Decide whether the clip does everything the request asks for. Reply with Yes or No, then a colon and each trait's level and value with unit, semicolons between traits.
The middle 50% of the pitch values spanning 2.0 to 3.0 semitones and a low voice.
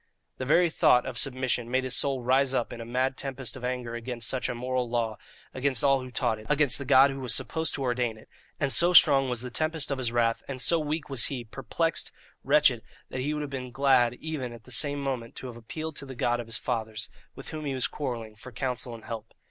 Yes: narrow, 2.6 semitones; low, 130 Hz